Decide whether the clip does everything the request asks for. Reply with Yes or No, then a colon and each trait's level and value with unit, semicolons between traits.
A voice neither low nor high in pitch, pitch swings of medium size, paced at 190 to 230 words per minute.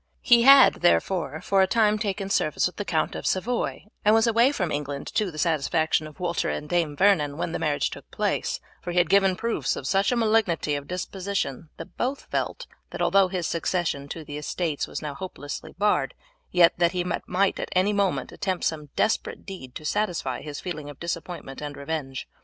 Yes: medium, 175 Hz; average, 4.7 semitones; average, 200 wpm